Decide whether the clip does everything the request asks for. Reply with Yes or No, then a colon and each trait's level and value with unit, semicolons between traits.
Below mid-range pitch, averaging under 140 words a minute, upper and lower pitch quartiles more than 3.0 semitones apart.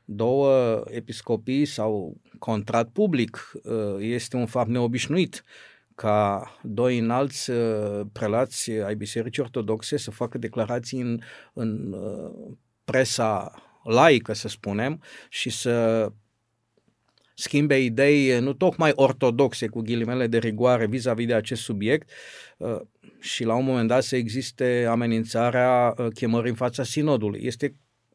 No: low, 120 Hz; slow, 115 wpm; narrow, 2.4 semitones